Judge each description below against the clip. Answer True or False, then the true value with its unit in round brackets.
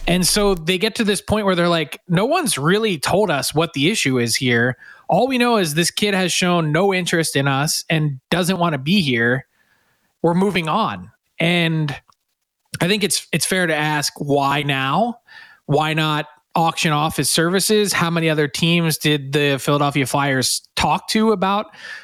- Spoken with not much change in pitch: False (4.9 semitones)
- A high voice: False (165 Hz)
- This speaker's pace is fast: False (185 wpm)